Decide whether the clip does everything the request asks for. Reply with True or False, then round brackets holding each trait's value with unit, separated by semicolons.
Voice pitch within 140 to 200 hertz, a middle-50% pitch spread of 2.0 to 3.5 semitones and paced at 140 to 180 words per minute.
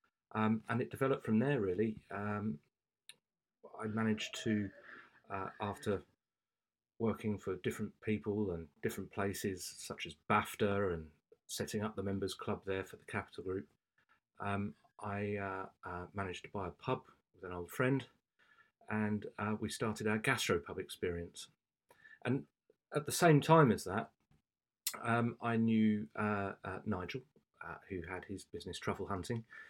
False (105 Hz; 2.4 semitones; 150 wpm)